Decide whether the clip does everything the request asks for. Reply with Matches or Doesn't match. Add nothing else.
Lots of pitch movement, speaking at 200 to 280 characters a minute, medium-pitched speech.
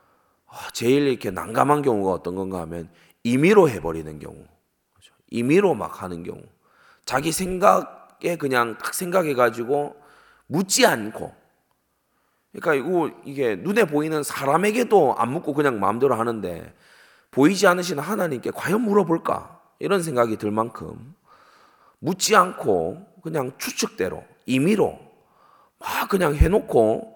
Matches